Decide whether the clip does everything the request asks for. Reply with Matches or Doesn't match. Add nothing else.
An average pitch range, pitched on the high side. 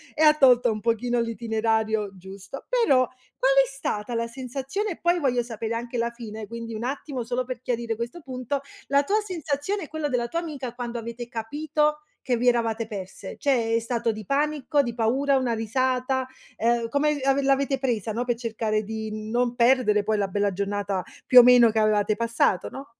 Matches